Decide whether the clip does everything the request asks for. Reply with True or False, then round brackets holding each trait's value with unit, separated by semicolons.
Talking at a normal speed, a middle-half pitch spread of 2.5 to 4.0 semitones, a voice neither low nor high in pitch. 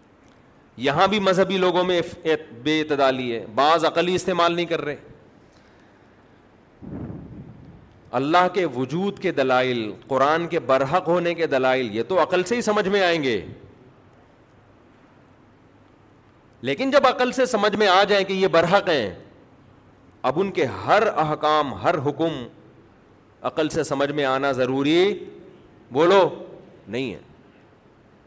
False (130 wpm; 5.6 semitones; 155 Hz)